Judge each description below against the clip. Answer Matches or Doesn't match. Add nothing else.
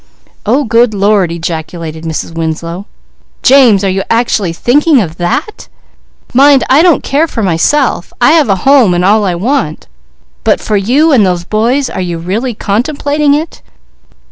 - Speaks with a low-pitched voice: Doesn't match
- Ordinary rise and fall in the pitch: Doesn't match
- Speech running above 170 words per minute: Doesn't match